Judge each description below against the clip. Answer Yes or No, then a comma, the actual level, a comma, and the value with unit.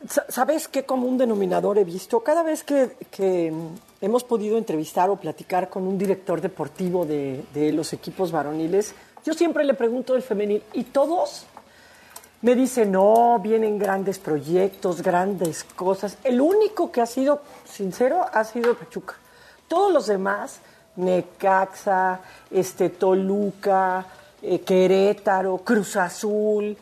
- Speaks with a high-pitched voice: Yes, high, 200 Hz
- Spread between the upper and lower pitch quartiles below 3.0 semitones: No, average, 4.6 semitones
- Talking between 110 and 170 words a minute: Yes, average, 130 wpm